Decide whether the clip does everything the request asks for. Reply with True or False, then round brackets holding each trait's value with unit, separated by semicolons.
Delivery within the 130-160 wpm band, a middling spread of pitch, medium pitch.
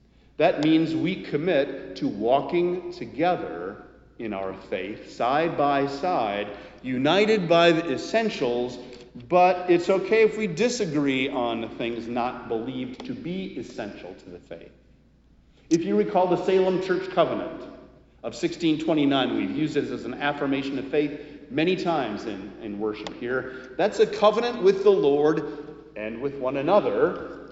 False (145 wpm; 6.6 semitones; 145 Hz)